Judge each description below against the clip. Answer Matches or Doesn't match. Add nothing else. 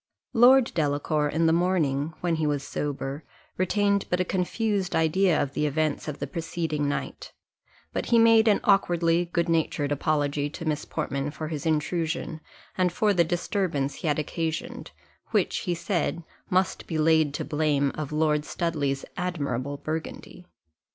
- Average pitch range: Matches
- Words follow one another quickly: Doesn't match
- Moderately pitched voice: Matches